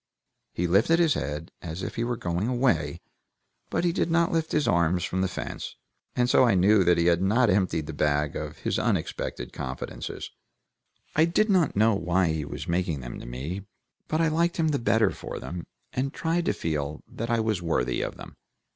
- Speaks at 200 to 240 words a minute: Yes, fast, 205 wpm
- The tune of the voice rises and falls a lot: Yes, wide, 7.7 semitones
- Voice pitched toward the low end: Yes, very low, 95 Hz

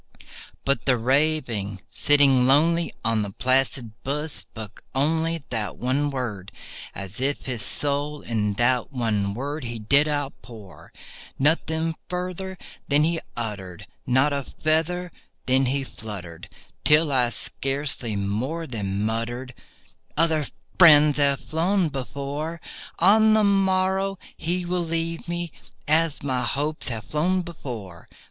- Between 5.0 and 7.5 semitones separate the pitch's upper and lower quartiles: Yes, wide, 5.5 semitones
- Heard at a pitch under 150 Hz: Yes, medium, 140 Hz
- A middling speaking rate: No, slow, 125 wpm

